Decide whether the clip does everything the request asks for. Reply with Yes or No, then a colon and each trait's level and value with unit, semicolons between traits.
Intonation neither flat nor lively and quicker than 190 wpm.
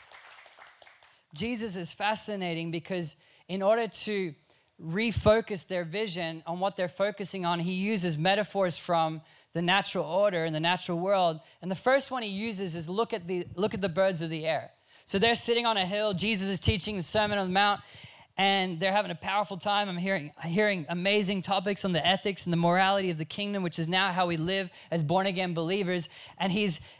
Yes: average, 3.0 semitones; average, 200 wpm